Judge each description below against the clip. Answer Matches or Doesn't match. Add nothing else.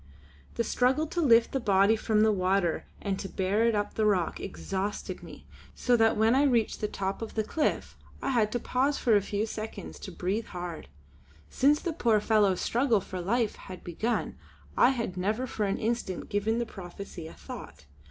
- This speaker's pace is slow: Doesn't match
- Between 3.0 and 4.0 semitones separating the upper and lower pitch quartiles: Matches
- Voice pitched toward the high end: Matches